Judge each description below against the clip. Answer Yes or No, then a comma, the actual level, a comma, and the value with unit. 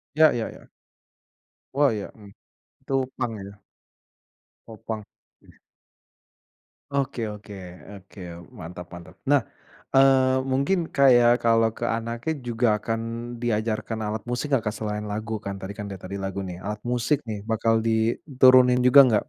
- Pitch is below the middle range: Yes, low, 115 Hz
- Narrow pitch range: No, average, 3.4 semitones